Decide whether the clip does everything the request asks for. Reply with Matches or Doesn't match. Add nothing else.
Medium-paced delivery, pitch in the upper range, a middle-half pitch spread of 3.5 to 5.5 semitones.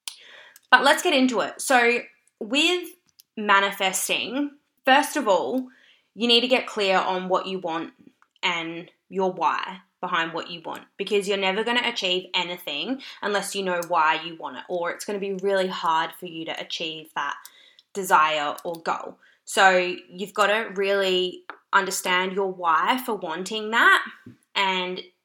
Matches